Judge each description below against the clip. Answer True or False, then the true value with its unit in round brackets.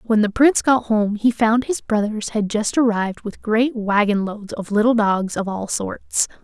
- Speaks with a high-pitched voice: True (220 Hz)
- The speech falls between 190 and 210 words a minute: True (205 wpm)